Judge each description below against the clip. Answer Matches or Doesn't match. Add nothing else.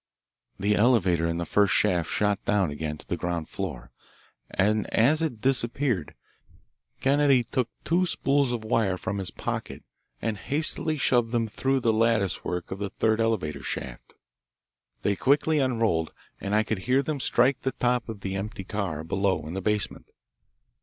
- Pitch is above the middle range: Doesn't match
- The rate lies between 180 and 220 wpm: Doesn't match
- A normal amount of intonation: Matches